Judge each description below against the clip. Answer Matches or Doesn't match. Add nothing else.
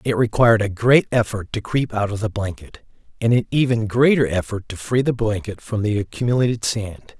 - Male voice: Matches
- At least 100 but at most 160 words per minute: Doesn't match